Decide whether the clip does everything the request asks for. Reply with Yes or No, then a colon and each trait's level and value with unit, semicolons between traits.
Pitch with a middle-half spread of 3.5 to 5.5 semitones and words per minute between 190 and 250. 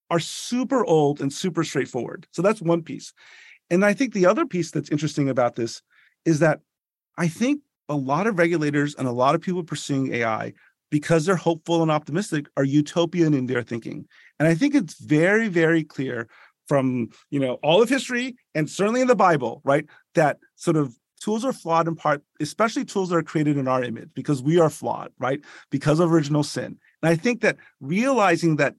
Yes: average, 4.0 semitones; average, 200 wpm